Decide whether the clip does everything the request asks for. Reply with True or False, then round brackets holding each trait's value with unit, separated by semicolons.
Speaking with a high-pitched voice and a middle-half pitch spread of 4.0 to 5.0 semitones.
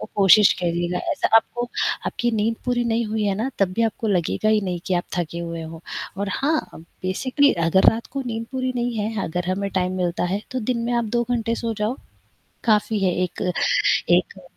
True (210 Hz; 4.5 semitones)